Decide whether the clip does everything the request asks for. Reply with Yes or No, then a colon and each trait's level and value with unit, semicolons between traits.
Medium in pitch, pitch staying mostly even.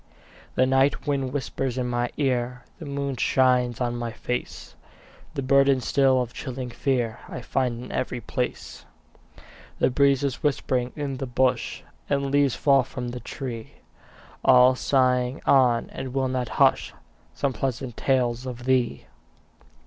No: low, 130 Hz; narrow, 1.7 semitones